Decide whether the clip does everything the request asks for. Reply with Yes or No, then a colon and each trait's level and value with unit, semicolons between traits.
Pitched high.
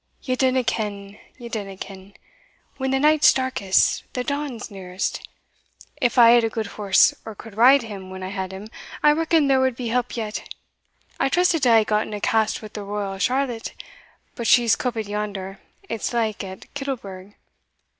Yes: high, 225 Hz